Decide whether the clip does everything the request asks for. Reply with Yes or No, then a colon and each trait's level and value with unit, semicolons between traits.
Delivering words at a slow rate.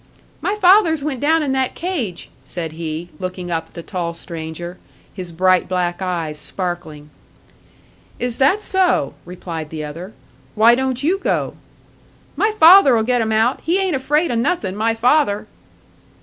No: average, 155 wpm